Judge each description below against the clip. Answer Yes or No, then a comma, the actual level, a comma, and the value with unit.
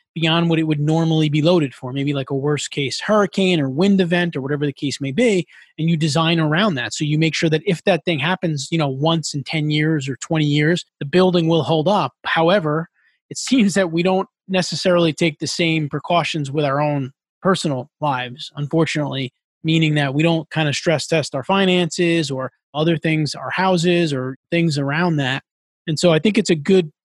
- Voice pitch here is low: No, medium, 160 Hz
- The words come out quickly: Yes, fast, 210 wpm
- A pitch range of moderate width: Yes, average, 3.0 semitones